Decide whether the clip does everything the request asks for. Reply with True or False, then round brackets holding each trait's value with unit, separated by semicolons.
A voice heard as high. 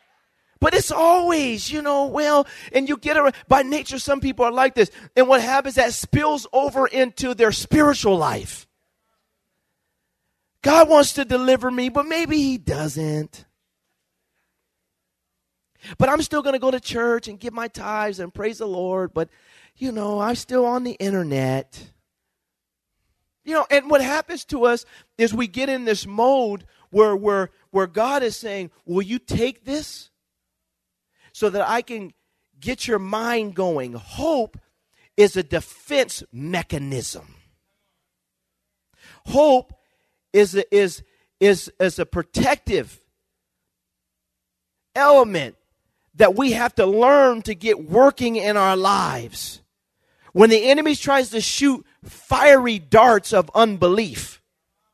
True (235 Hz)